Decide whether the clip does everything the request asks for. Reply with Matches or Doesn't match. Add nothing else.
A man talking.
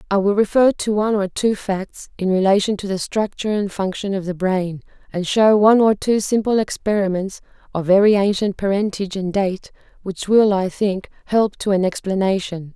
Doesn't match